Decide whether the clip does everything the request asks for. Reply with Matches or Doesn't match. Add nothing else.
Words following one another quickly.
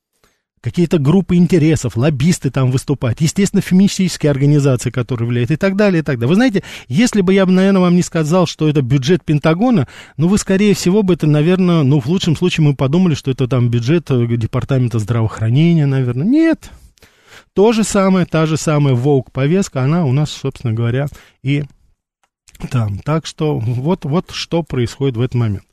Matches